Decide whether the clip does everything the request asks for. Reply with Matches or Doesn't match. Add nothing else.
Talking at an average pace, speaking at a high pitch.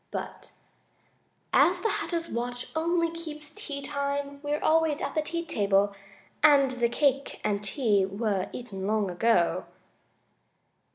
Doesn't match